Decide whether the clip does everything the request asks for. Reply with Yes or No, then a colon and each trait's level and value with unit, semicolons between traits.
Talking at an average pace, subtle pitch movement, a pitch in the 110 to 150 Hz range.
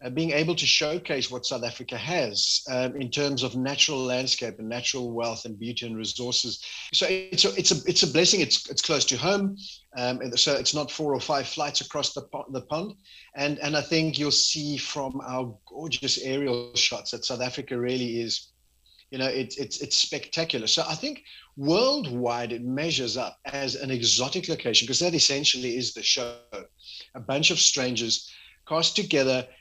No: average, 190 wpm; average, 3.5 semitones; low, 135 Hz